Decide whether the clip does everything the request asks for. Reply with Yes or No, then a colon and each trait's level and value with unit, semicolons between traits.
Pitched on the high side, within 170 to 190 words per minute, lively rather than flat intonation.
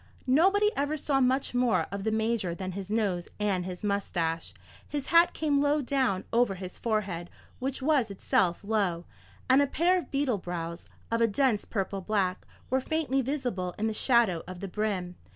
Yes: high, 220 Hz; average, 180 wpm; wide, 6.4 semitones